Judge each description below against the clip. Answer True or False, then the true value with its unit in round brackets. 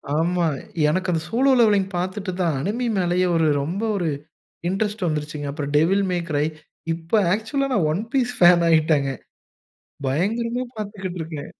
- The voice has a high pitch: False (180 Hz)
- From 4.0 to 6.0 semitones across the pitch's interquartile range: True (4.6 semitones)